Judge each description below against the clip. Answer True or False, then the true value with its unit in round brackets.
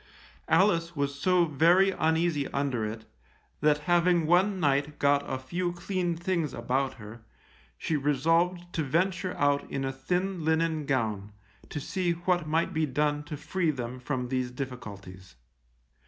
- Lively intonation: False (4.6 semitones)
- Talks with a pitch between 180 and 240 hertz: False (150 Hz)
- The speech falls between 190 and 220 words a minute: False (150 wpm)